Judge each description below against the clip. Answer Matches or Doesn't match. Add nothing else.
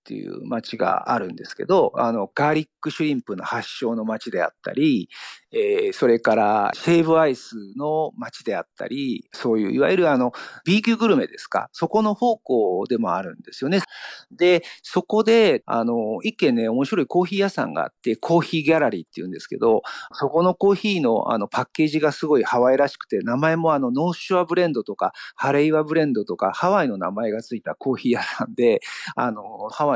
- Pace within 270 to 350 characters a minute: Doesn't match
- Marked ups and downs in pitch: Matches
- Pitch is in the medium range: Matches